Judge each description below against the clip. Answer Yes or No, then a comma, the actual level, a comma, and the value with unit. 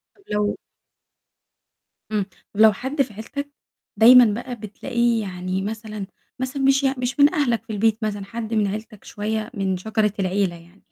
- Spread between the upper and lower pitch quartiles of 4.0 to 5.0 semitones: No, average, 3.3 semitones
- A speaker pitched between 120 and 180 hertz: No, high, 220 Hz